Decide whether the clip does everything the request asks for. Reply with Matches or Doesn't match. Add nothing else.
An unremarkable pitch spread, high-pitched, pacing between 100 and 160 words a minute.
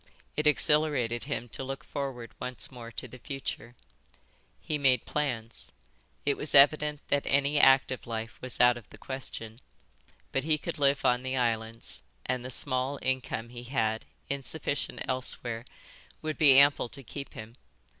Doesn't match